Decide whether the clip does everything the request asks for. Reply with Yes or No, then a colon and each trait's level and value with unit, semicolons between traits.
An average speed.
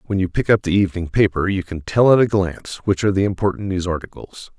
No: fast, 250 wpm